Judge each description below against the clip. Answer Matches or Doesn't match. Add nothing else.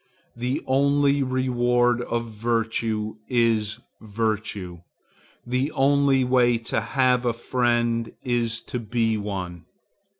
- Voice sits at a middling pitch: Doesn't match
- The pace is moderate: Doesn't match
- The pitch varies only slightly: Matches